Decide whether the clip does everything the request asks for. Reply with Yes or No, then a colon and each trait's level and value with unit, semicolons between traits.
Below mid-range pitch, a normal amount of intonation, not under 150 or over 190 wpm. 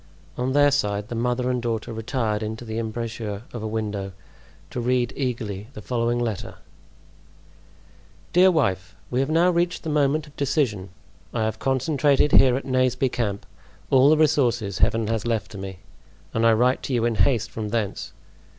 Yes: low, 120 Hz; average, 3.5 semitones; average, 170 wpm